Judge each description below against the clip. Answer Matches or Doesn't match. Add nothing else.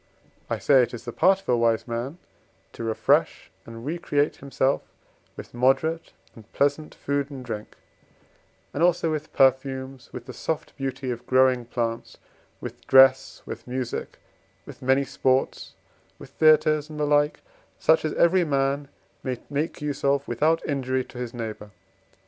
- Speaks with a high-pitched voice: Doesn't match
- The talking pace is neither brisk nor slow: Matches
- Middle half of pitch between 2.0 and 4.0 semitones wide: Matches